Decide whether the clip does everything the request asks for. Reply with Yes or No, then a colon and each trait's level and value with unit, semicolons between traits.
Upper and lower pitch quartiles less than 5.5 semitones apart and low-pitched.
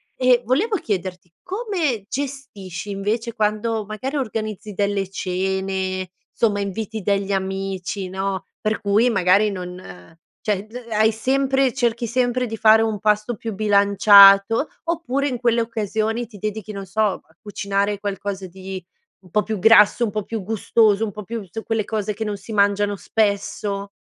No: narrow, 2.4 semitones; high, 210 Hz